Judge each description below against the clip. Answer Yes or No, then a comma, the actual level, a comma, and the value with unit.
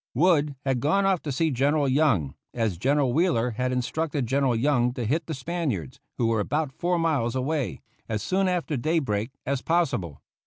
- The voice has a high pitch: No, medium, 140 Hz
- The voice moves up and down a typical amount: Yes, average, 4.9 semitones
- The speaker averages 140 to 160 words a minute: No, average, 180 wpm